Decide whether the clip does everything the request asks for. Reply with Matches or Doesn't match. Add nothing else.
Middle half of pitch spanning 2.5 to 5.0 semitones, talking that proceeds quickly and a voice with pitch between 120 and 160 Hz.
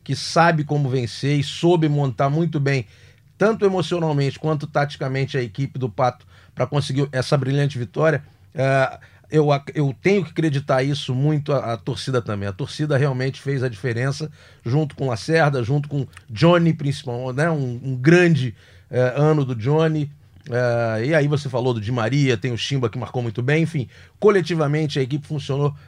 Doesn't match